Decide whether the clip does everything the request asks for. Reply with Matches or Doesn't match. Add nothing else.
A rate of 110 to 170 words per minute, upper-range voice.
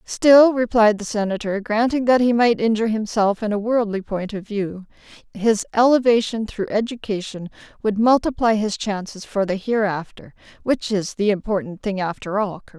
Matches